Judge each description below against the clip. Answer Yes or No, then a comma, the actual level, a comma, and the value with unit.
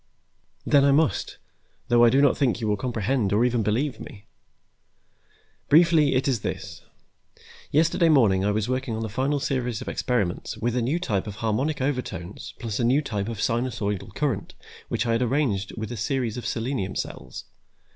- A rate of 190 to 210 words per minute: No, average, 180 wpm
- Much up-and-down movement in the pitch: No, average, 4.3 semitones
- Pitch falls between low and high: No, low, 120 Hz